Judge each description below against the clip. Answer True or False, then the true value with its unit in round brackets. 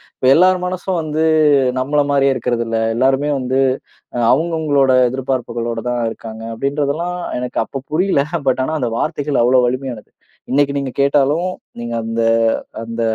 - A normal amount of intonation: True (3.3 semitones)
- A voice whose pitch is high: False (135 Hz)